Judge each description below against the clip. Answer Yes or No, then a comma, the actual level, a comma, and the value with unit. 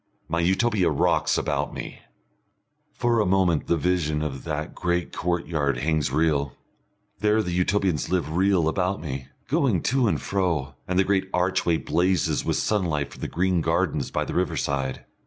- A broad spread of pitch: No, average, 3.7 semitones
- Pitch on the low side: Yes, very low, 85 Hz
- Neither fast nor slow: Yes, average, 160 wpm